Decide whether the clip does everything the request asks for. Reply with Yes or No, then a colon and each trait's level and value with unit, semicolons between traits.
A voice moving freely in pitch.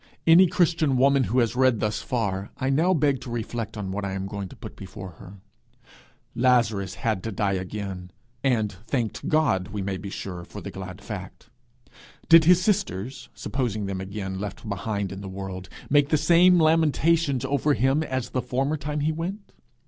Yes: wide, 6.9 semitones